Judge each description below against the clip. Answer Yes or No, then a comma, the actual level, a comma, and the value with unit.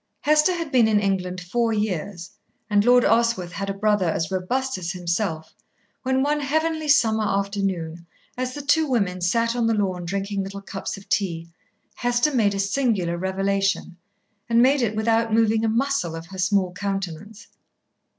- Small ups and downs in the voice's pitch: No, average, 4.4 semitones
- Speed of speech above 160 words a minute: Yes, average, 170 wpm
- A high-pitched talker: Yes, high, 205 Hz